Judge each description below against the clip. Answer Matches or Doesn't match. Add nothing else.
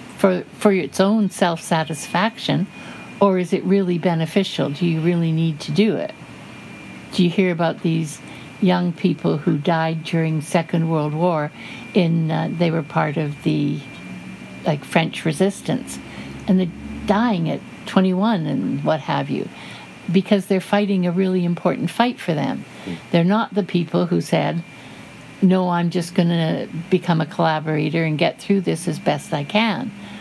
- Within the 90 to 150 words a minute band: Doesn't match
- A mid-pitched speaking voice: Matches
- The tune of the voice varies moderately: Matches